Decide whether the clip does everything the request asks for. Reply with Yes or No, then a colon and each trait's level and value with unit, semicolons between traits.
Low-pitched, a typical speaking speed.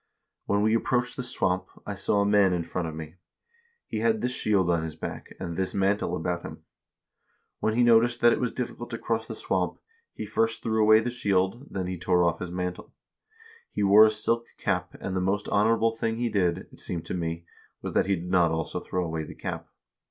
No: low, 100 Hz; fast, 225 wpm